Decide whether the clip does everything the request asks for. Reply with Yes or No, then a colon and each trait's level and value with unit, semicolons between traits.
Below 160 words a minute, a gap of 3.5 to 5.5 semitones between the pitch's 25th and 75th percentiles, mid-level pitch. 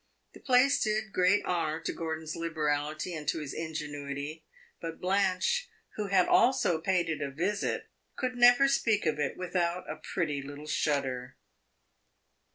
Yes: average, 150 wpm; average, 4.7 semitones; medium, 165 Hz